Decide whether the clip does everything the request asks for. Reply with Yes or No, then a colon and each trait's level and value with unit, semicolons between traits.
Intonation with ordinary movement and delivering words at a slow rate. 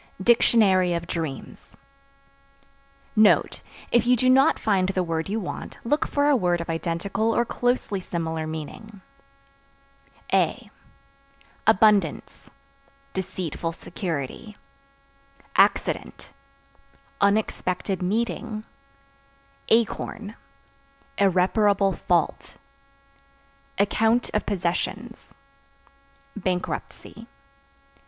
Yes: average, 4.1 semitones; slow, 80 wpm